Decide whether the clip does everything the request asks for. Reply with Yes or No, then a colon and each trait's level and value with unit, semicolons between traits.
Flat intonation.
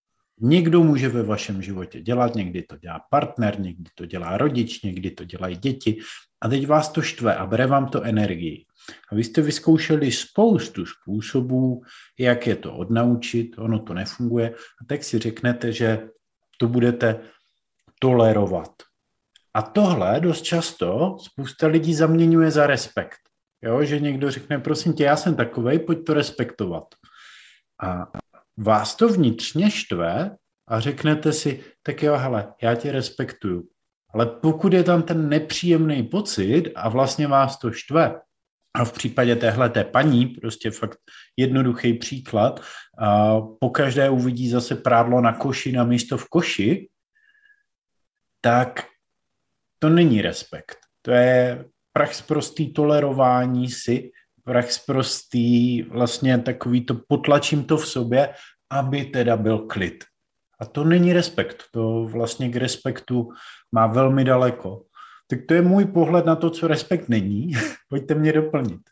No: average, 4.8 semitones